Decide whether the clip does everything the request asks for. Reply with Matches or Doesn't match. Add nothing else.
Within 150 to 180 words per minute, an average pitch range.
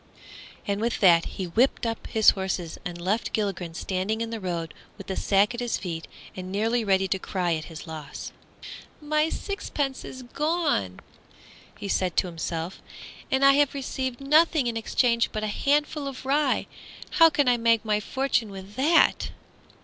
Doesn't match